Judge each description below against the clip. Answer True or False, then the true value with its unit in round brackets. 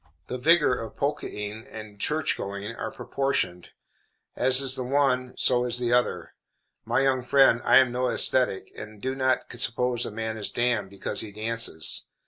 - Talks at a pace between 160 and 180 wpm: True (170 wpm)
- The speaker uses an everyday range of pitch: True (3.2 semitones)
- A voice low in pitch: True (125 Hz)